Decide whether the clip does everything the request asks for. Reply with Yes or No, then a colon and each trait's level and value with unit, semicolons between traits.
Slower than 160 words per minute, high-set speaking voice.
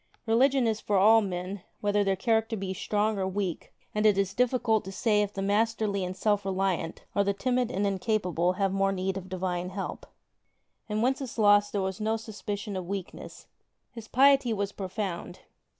No: average, 180 wpm; high, 205 Hz